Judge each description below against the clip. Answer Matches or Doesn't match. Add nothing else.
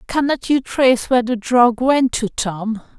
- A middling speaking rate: Matches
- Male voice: Doesn't match